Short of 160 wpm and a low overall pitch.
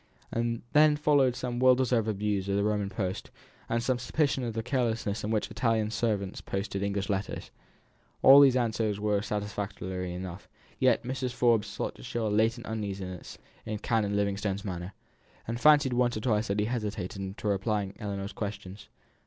No: average, 175 wpm; low, 105 Hz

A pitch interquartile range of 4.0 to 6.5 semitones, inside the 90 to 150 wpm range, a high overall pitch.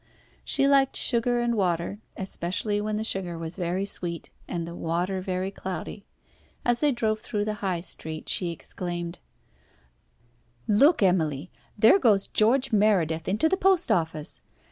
Yes: average, 4.4 semitones; average, 145 wpm; high, 195 Hz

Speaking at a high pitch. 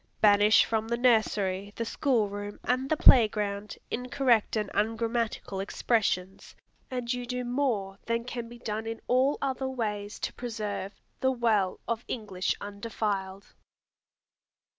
Yes: high, 225 Hz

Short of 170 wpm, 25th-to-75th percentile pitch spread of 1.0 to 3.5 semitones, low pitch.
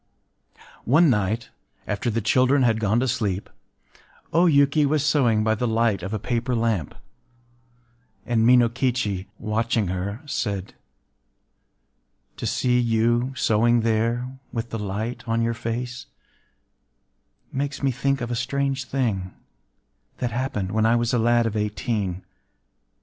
Yes: slow, 135 wpm; average, 2.8 semitones; low, 115 Hz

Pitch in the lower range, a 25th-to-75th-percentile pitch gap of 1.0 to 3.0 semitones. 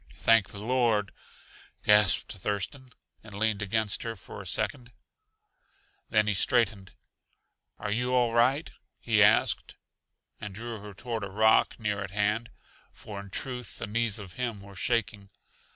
Yes: low, 110 Hz; narrow, 2.6 semitones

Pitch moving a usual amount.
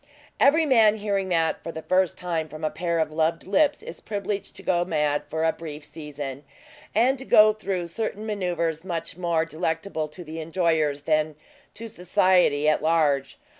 Yes: average, 4.1 semitones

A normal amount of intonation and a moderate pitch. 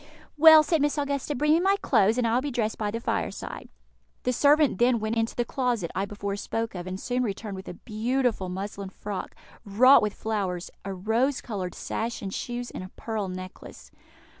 No: average, 4.4 semitones; high, 225 Hz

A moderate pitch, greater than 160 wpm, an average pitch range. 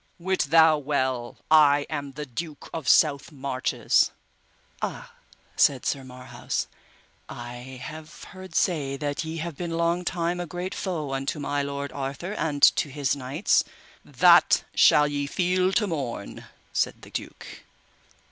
No: medium, 150 Hz; average, 145 wpm; average, 3.4 semitones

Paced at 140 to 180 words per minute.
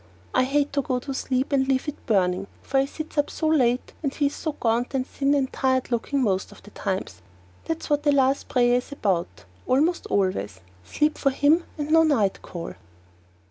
No: average, 195 wpm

